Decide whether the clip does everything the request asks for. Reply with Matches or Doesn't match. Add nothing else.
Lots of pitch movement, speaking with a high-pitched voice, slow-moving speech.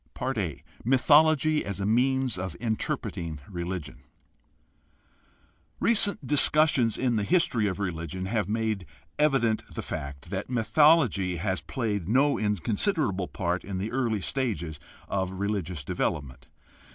Doesn't match